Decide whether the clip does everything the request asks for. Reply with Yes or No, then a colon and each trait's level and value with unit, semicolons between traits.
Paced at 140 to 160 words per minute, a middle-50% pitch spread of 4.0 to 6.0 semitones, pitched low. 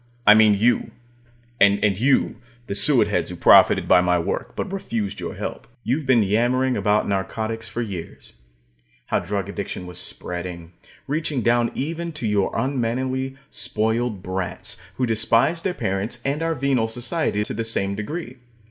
Yes: average, 155 wpm; average, 4.6 semitones; low, 115 Hz